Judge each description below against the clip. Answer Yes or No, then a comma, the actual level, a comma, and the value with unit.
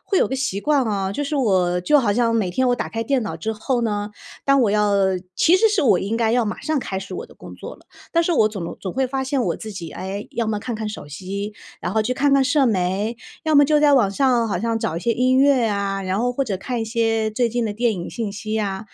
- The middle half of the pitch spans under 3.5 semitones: No, average, 4.6 semitones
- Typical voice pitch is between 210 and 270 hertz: Yes, high, 225 Hz